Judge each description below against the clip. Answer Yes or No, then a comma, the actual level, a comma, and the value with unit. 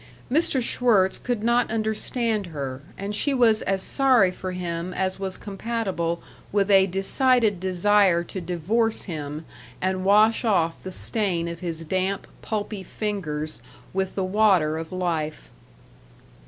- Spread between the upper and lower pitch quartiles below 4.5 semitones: Yes, average, 4.0 semitones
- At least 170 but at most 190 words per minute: No, average, 140 wpm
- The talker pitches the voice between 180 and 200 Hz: Yes, high, 190 Hz